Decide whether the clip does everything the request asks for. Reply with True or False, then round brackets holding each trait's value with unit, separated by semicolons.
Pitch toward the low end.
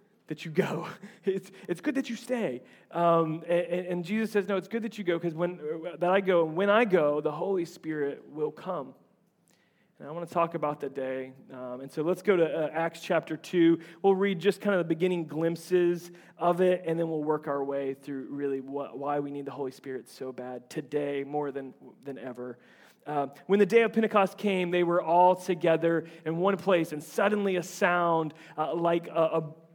False (170 Hz)